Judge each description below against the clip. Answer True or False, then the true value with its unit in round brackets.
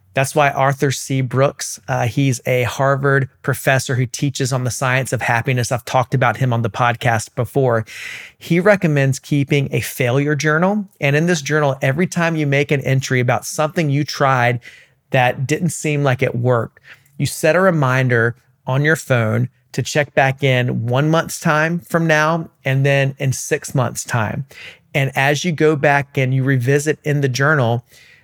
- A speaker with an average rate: True (180 wpm)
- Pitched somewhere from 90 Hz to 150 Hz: True (135 Hz)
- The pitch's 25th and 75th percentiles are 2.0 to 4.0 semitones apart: True (2.9 semitones)